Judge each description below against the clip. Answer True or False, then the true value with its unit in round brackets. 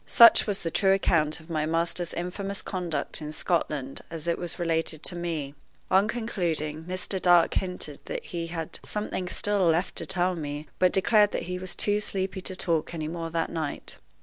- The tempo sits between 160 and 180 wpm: False (190 wpm)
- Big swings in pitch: False (2.8 semitones)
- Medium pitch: True (175 Hz)